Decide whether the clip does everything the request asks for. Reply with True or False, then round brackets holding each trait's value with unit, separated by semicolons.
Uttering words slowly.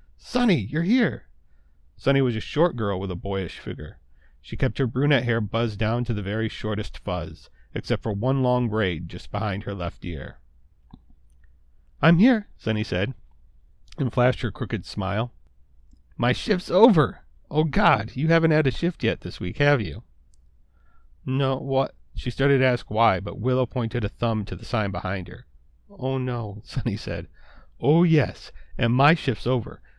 False (170 wpm)